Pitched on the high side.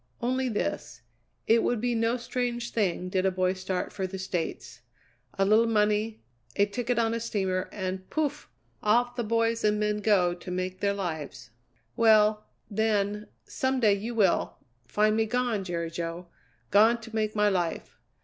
Yes: high, 210 Hz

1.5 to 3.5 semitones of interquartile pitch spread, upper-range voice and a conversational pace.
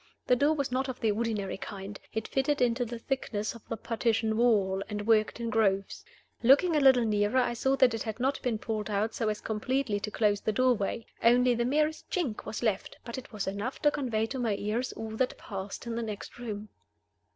No: average, 3.1 semitones; high, 230 Hz; fast, 220 wpm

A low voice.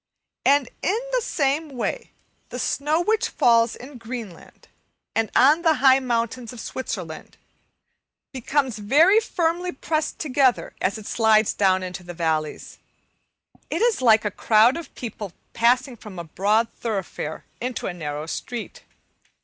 No: high, 240 Hz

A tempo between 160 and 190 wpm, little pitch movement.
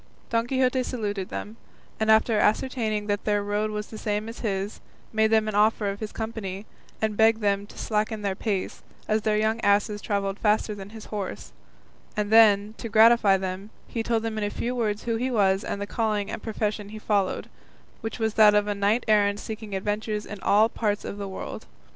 No: fast, 205 wpm; narrow, 1.4 semitones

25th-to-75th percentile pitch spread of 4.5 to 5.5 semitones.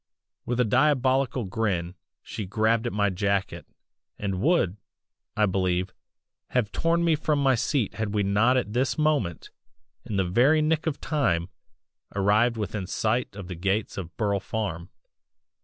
Yes: average, 5.1 semitones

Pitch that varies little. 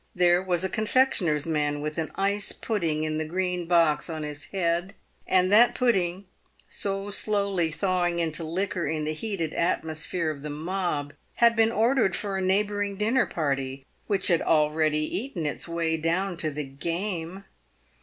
No: average, 4.1 semitones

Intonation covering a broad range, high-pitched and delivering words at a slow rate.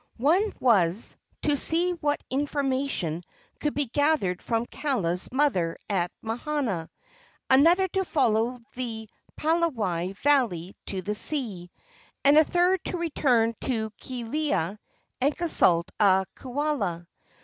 Yes: wide, 7.1 semitones; very high, 255 Hz; slow, 115 wpm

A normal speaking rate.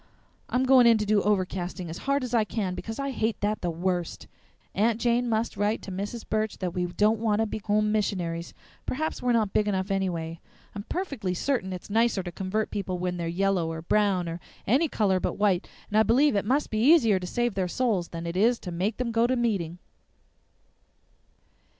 No: fast, 210 wpm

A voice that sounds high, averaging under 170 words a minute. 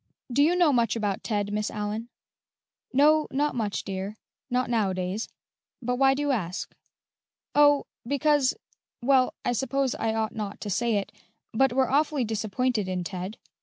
Yes: high, 235 Hz; average, 160 wpm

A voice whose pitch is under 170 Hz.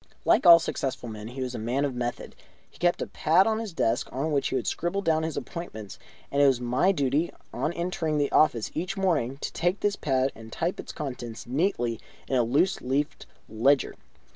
Yes: medium, 140 Hz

